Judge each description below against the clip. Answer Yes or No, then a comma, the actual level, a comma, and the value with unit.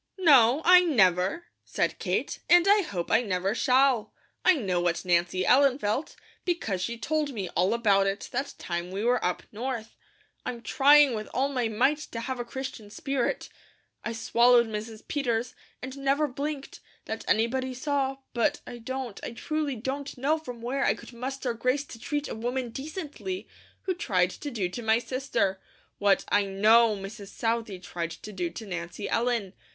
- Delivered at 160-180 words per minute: Yes, average, 175 wpm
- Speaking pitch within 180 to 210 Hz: No, high, 240 Hz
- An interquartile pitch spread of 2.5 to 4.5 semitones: No, average, 5.0 semitones